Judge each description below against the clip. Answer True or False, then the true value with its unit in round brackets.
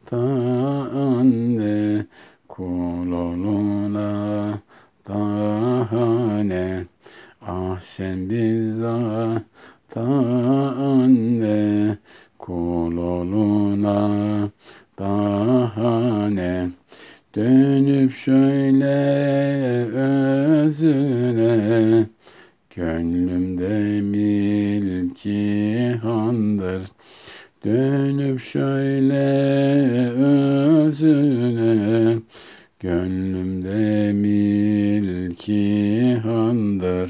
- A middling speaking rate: False (35 wpm)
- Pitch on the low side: True (110 Hz)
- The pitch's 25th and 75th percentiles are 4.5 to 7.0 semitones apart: False (3.9 semitones)